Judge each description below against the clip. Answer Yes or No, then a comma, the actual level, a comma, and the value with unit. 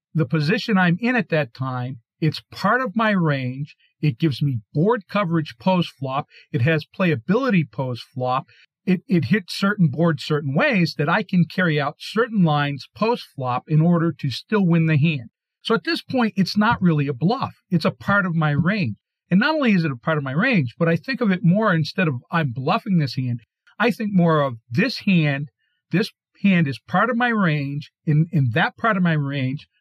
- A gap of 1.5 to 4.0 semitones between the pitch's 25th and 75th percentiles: No, wide, 5.5 semitones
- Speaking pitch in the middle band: Yes, medium, 165 Hz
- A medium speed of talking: No, fast, 210 wpm